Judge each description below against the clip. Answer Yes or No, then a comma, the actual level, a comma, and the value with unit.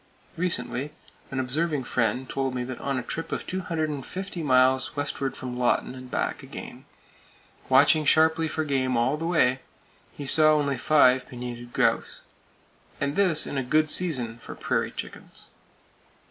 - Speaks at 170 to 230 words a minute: No, average, 150 wpm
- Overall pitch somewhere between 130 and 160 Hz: Yes, medium, 140 Hz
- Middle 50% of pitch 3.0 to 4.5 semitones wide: Yes, average, 3.4 semitones